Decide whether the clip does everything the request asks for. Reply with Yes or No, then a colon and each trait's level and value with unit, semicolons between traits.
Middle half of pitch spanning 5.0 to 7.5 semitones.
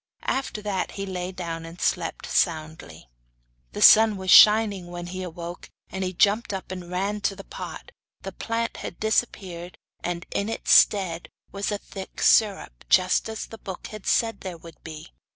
No: average, 3.2 semitones